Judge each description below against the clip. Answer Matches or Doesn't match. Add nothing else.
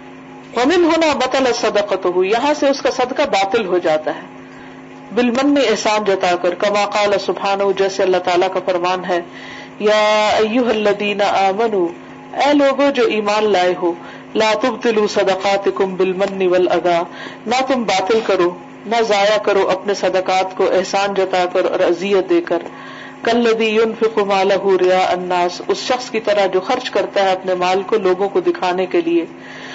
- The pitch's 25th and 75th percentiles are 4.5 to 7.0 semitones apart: Doesn't match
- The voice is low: Doesn't match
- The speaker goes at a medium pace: Matches